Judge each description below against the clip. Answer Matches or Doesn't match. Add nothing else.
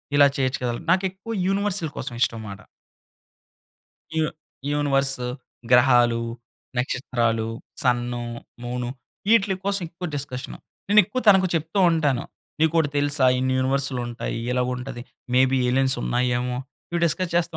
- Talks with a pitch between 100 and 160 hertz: Matches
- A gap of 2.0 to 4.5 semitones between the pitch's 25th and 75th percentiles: Doesn't match